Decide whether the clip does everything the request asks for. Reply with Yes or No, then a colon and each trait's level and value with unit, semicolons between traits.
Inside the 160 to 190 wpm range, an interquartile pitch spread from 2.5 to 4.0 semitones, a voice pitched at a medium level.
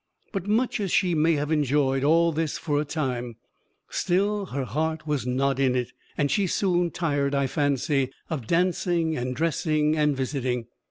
Yes: average, 170 wpm; average, 3.7 semitones; medium, 150 Hz